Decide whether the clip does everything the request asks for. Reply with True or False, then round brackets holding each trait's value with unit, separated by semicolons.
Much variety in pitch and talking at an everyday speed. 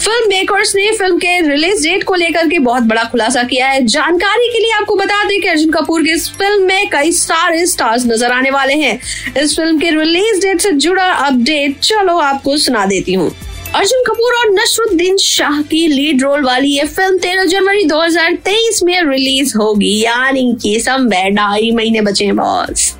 True (6.6 semitones; 180 wpm)